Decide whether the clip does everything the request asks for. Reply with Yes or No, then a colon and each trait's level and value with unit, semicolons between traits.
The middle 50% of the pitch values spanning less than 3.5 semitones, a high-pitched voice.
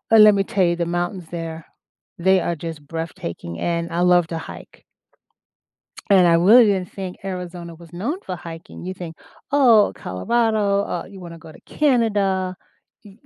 No: average, 3.0 semitones; medium, 180 Hz